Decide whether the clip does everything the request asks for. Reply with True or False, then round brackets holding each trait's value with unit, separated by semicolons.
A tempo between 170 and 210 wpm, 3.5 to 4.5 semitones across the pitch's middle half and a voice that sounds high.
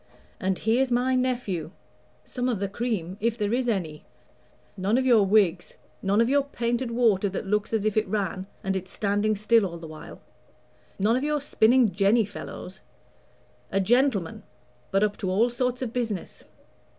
True (175 wpm; 3.9 semitones; 215 Hz)